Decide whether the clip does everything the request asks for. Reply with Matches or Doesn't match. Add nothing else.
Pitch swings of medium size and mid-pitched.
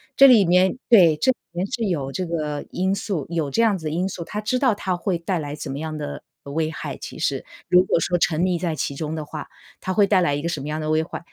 Matches